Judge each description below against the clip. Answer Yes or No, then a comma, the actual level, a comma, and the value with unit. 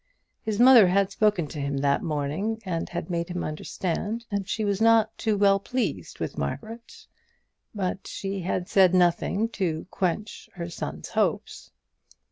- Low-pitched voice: No, high, 195 Hz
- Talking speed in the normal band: Yes, average, 150 wpm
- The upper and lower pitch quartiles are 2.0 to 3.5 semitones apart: No, average, 3.9 semitones